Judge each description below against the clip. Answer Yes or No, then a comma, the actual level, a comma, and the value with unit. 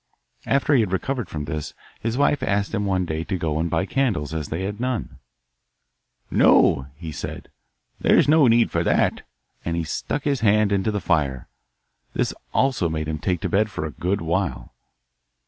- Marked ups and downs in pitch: Yes, wide, 6.2 semitones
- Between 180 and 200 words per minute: Yes, average, 185 wpm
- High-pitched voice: No, very low, 95 Hz